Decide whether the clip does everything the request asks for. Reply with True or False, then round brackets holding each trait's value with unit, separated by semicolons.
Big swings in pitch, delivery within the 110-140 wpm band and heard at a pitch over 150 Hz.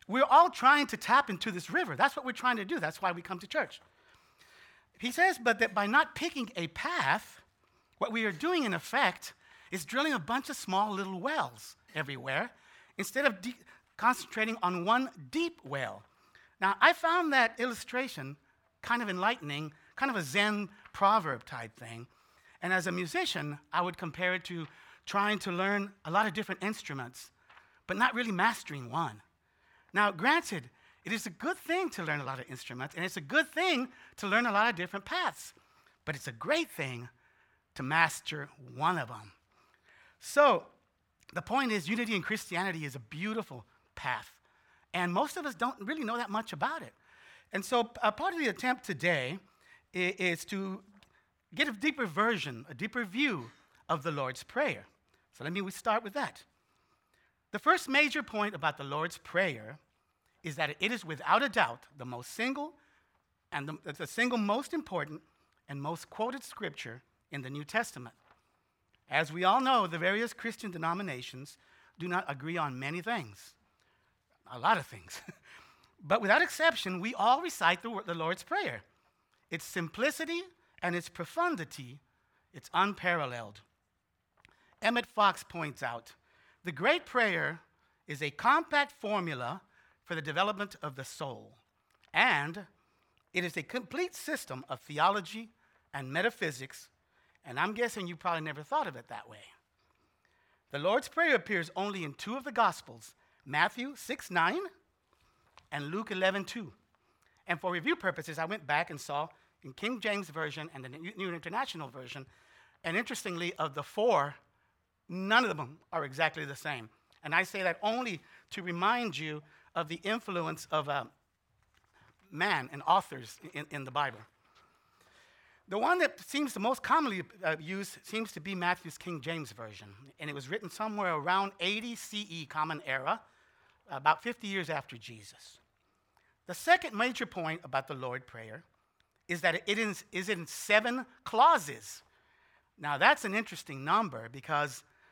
False (7.3 semitones; 165 wpm; 185 Hz)